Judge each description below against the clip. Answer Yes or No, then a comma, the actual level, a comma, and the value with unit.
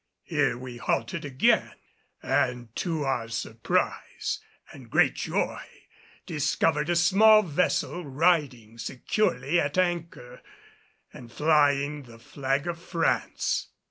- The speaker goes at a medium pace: No, slow, 110 wpm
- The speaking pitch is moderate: Yes, medium, 145 Hz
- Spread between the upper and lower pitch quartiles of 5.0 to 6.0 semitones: Yes, wide, 5.5 semitones